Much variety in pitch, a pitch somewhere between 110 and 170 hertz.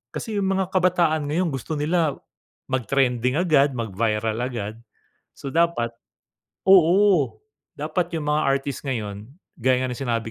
Yes: wide, 6.0 semitones; medium, 140 Hz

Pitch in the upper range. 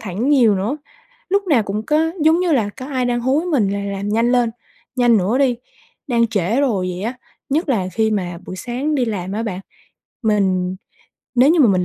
Yes: high, 230 Hz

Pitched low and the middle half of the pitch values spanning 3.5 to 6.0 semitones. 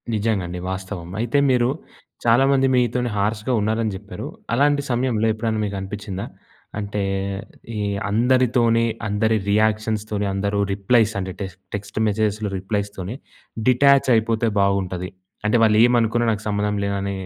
No: low, 110 Hz; average, 2.8 semitones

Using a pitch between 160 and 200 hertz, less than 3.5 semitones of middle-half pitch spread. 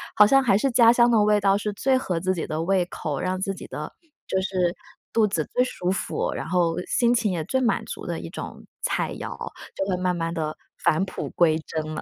No: high, 190 Hz; average, 4.2 semitones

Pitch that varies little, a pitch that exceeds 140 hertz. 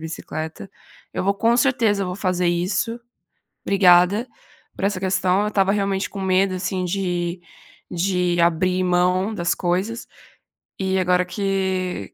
Yes: narrow, 1.7 semitones; medium, 185 Hz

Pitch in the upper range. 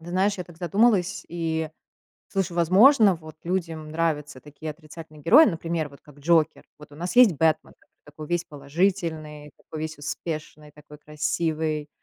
No: medium, 160 Hz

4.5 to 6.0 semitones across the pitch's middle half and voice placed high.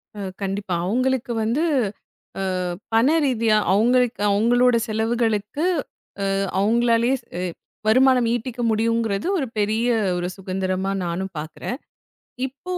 No: average, 3.7 semitones; high, 230 Hz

